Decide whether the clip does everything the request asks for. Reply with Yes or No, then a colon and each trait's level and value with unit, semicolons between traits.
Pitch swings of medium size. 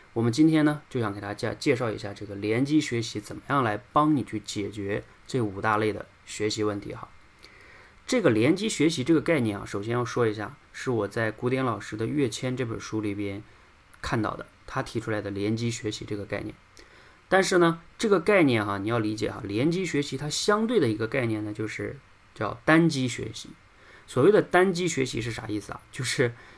Yes: average, 4.9 semitones